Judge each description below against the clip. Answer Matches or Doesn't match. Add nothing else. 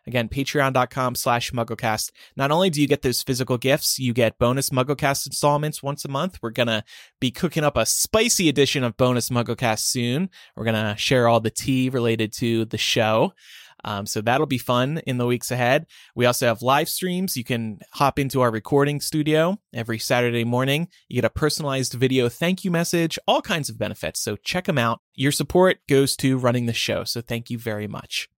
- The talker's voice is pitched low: Matches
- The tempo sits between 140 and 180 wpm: Doesn't match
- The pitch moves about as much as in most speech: Matches